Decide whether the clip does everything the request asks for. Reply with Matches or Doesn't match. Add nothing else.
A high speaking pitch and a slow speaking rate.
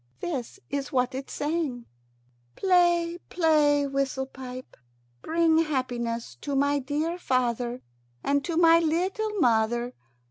Matches